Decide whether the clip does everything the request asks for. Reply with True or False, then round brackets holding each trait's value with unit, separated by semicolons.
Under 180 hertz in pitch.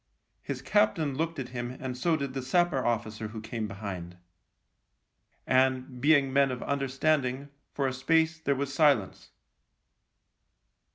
True (135 Hz)